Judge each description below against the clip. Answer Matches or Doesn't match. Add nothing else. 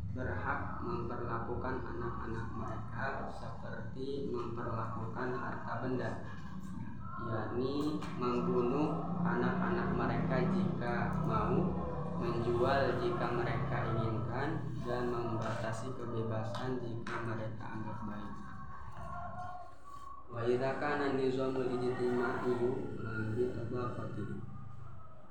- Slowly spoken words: Matches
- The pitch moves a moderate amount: Matches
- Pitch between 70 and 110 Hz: Doesn't match